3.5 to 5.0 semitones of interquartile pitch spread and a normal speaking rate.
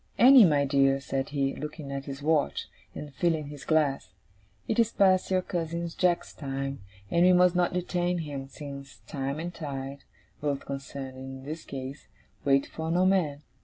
Yes: average, 4.0 semitones; average, 170 wpm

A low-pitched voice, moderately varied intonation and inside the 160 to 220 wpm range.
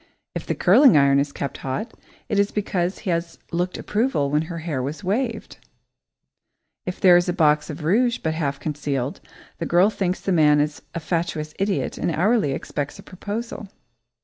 No: medium, 170 Hz; average, 5.0 semitones; average, 180 wpm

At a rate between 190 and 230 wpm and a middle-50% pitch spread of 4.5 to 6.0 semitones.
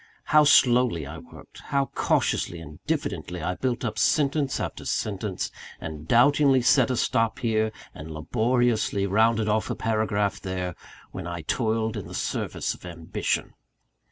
No: average, 150 wpm; wide, 5.6 semitones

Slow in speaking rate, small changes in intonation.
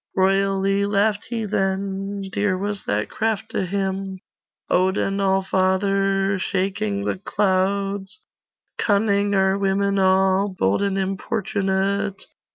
Yes: slow, 105 wpm; narrow, 0.8 semitones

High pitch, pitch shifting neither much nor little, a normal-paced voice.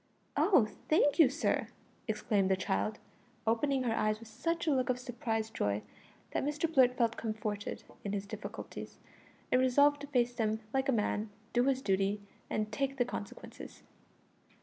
Yes: high, 235 Hz; average, 4.2 semitones; average, 165 wpm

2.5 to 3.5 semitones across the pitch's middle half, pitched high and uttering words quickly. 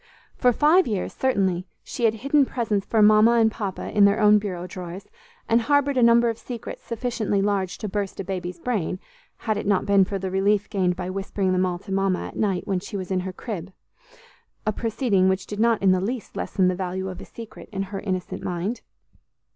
Yes: average, 3.2 semitones; high, 200 Hz; fast, 215 wpm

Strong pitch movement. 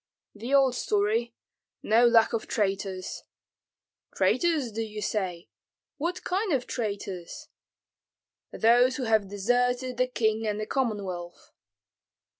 No: average, 3.5 semitones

